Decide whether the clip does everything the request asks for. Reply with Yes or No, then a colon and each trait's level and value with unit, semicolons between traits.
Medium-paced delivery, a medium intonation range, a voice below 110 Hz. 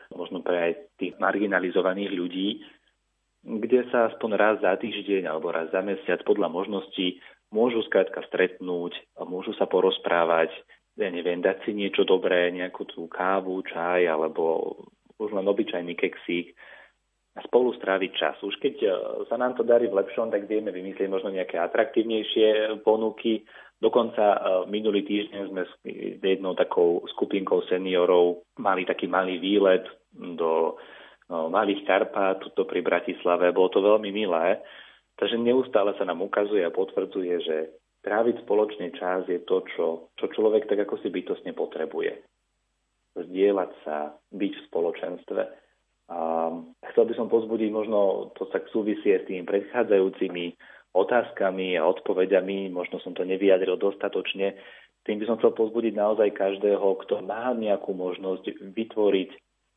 Yes: average, 145 wpm; average, 4.8 semitones; low, 100 Hz